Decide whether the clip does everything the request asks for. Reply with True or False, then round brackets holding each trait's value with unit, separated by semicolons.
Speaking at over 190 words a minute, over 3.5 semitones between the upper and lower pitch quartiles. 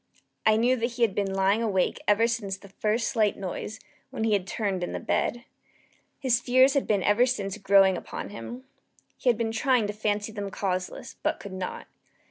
False (200 wpm; 3.1 semitones)